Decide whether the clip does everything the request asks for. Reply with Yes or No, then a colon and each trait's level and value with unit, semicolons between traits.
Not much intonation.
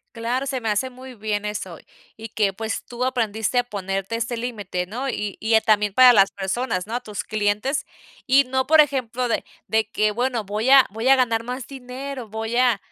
No: average, 3.4 semitones